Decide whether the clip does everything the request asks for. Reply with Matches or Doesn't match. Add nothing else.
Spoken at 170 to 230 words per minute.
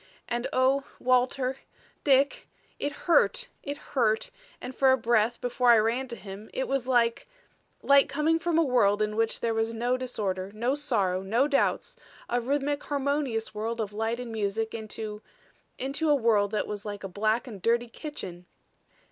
Matches